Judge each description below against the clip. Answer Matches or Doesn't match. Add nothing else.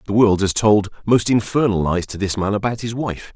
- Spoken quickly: Matches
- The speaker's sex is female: Doesn't match